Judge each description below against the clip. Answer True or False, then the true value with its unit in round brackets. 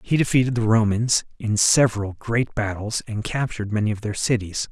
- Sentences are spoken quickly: False (180 wpm)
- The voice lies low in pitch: True (110 Hz)